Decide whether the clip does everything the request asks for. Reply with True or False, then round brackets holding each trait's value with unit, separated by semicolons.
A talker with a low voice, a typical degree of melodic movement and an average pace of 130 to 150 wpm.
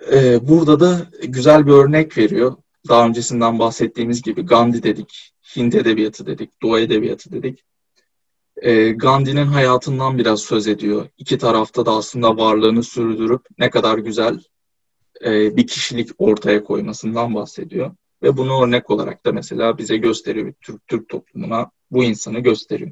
True (120 Hz; 3.0 semitones; 135 wpm)